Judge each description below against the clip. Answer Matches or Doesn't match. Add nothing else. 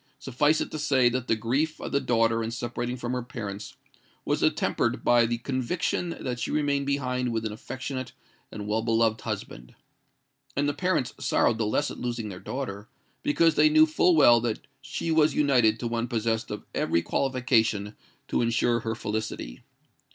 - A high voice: Doesn't match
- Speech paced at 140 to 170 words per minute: Doesn't match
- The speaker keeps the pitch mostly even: Doesn't match